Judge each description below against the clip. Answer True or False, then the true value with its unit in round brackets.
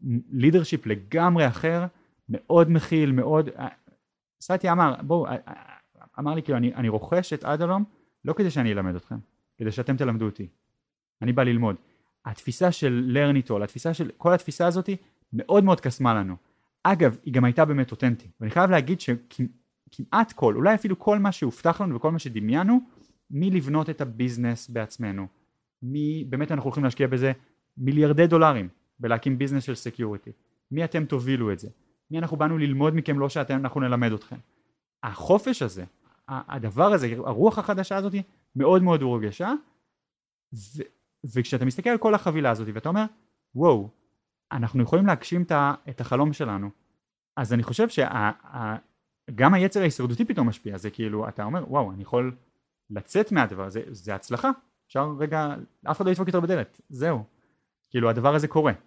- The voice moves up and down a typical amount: False (5.9 semitones)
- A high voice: False (140 Hz)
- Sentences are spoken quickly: True (155 wpm)